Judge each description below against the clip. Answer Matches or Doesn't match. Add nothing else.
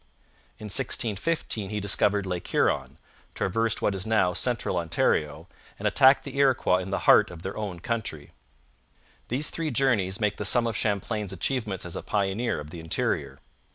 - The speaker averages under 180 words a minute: Matches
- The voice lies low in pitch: Matches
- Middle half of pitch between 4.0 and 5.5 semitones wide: Matches